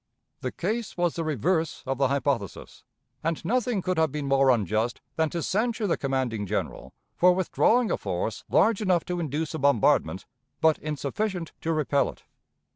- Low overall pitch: No, medium, 160 Hz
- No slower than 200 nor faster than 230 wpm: No, average, 170 wpm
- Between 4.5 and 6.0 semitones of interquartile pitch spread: Yes, average, 5.1 semitones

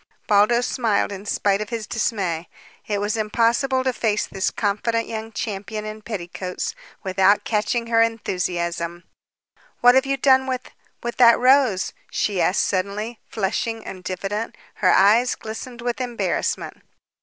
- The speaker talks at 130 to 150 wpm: Yes, average, 145 wpm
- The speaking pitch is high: Yes, high, 220 Hz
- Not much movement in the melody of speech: No, average, 3.2 semitones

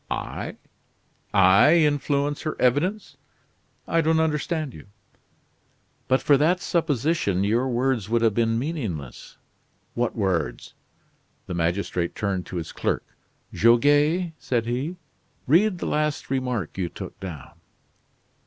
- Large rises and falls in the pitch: Yes, wide, 7.2 semitones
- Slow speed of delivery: Yes, slow, 120 wpm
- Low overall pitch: Yes, low, 130 Hz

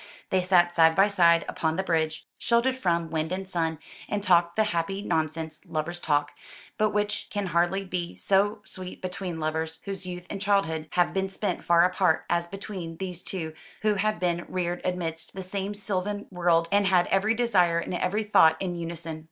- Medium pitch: Yes, medium, 180 Hz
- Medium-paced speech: Yes, average, 185 wpm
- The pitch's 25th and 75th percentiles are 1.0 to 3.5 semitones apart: Yes, average, 2.9 semitones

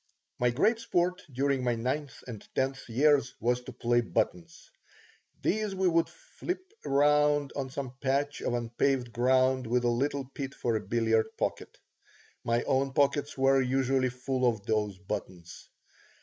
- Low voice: Yes, low, 130 Hz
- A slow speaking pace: No, average, 150 wpm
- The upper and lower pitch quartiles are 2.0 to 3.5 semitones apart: Yes, average, 3.1 semitones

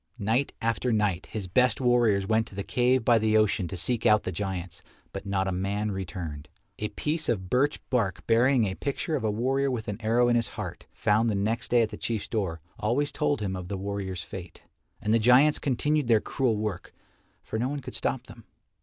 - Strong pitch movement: No, average, 3.9 semitones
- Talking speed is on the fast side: Yes, fast, 215 wpm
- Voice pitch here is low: Yes, low, 110 Hz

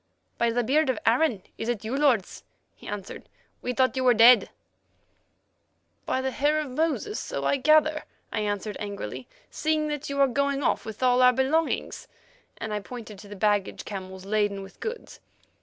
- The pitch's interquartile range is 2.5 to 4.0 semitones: No, average, 5.2 semitones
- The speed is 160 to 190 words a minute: Yes, average, 180 wpm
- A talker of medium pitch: No, very high, 250 Hz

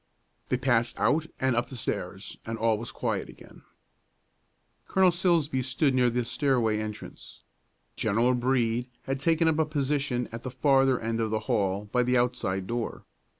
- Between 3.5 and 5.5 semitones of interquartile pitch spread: No, average, 3.1 semitones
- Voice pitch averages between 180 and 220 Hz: No, low, 125 Hz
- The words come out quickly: No, average, 165 wpm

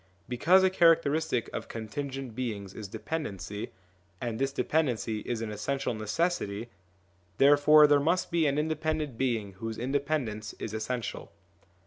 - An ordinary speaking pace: No, slow, 130 wpm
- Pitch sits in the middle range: No, low, 130 Hz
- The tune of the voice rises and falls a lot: Yes, wide, 5.7 semitones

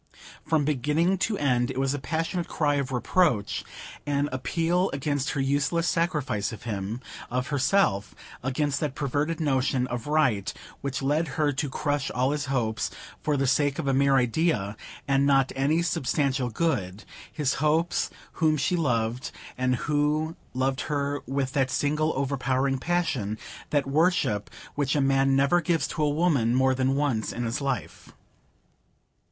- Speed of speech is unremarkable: Yes, average, 155 wpm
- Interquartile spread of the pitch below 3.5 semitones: Yes, average, 2.9 semitones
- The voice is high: No, medium, 140 Hz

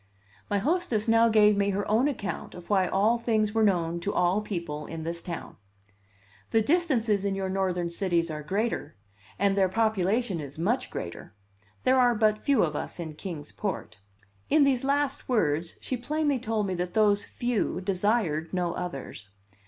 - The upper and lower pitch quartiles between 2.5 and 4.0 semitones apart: No, average, 4.6 semitones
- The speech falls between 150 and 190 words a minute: Yes, average, 175 wpm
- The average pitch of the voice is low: No, high, 200 Hz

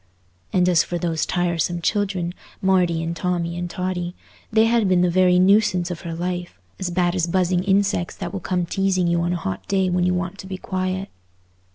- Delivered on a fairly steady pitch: Yes, narrow, 1.5 semitones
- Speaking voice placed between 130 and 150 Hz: No, medium, 180 Hz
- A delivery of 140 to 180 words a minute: No, average, 200 wpm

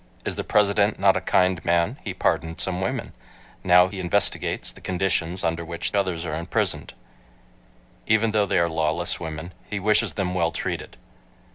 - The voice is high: No, very low, 90 Hz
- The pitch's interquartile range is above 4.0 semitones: No, average, 2.8 semitones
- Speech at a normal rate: Yes, average, 165 wpm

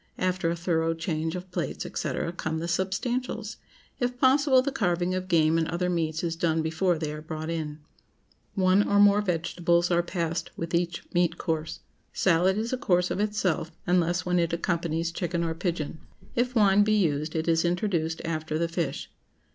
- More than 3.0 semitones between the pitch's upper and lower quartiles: No, narrow, 2.5 semitones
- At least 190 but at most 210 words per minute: No, average, 180 wpm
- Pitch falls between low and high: Yes, medium, 170 Hz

